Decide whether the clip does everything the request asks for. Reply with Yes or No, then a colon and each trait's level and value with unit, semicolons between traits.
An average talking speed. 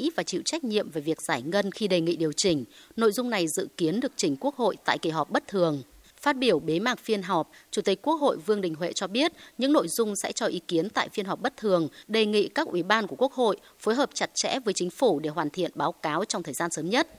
No: fast, 275 wpm